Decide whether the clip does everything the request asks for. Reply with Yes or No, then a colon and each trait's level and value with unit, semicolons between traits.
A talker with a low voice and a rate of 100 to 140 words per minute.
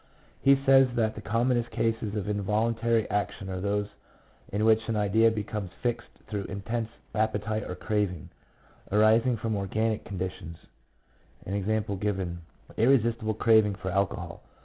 Yes: low, 110 Hz; slow, 135 wpm